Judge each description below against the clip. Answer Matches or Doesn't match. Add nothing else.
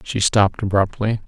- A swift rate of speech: Doesn't match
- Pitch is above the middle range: Doesn't match